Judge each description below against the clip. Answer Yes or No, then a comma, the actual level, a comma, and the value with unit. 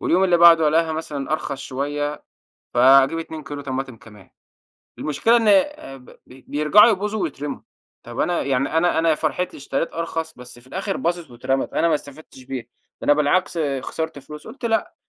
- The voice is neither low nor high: Yes, medium, 155 Hz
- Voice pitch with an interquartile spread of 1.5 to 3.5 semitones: No, average, 4.1 semitones